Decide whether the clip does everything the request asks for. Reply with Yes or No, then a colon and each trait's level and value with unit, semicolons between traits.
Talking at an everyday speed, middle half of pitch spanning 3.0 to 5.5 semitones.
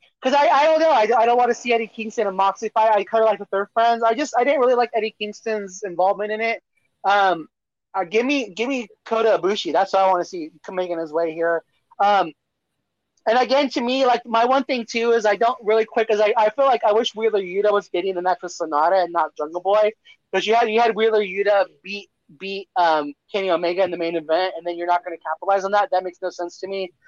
No: fast, 260 wpm; average, 3.7 semitones